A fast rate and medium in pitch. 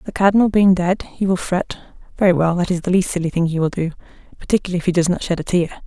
Yes: fast, 265 wpm; medium, 180 Hz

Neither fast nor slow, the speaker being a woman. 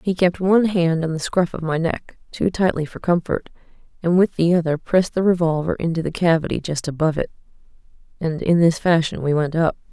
Yes: average, 195 wpm; female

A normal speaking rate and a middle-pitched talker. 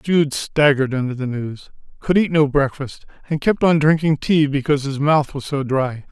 Yes: average, 195 wpm; medium, 145 Hz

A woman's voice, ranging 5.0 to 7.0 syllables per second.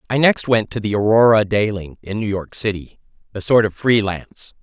No: male; 5.3 syllables/s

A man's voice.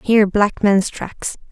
No: female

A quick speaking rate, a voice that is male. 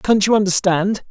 No: average, 165 wpm; male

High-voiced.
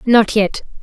Yes: high, 215 Hz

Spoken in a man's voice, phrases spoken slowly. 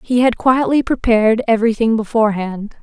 No: female; slow, 125 wpm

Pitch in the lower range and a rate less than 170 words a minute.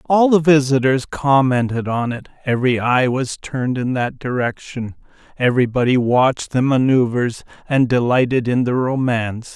Yes: low, 130 Hz; average, 140 wpm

